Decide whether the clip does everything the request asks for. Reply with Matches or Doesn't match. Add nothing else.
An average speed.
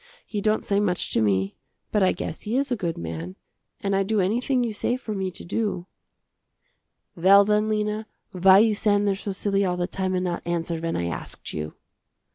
Doesn't match